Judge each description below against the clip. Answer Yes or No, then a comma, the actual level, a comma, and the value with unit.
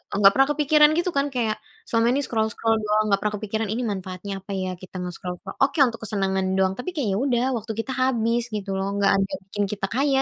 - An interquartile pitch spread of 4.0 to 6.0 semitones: Yes, average, 4.6 semitones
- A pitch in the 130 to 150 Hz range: No, high, 220 Hz